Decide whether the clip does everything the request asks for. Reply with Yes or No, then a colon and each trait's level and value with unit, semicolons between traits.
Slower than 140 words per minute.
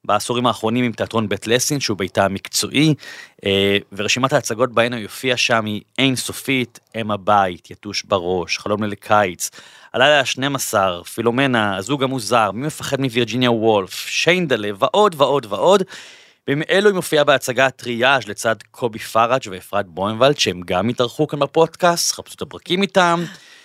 No: average, 145 wpm